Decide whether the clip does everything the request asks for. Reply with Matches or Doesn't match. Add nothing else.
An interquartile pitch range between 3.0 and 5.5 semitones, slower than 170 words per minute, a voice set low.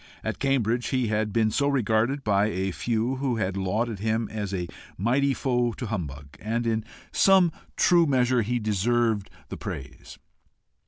Matches